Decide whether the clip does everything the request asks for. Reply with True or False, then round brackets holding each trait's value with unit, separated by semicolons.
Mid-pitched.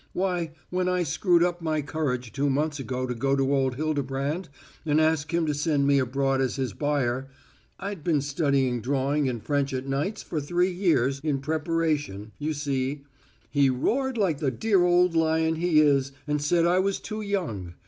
True (145 Hz)